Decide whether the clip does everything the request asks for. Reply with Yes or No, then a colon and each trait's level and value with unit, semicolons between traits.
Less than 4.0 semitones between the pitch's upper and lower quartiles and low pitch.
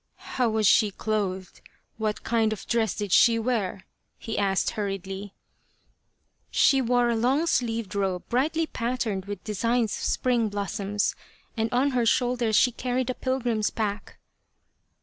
No: average, 3.3 semitones; high, 225 Hz